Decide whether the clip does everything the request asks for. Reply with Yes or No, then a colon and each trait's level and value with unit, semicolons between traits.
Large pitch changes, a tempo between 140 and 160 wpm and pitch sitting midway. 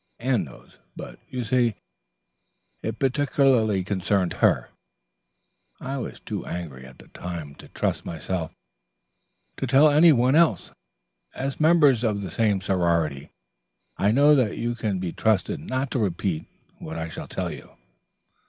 No: wide, 6.7 semitones; average, 145 wpm; low, 110 Hz